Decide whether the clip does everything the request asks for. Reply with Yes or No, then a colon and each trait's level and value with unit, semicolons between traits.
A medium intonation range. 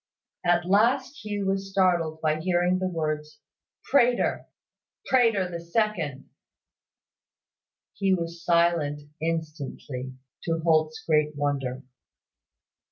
Yes: average, 3.9 semitones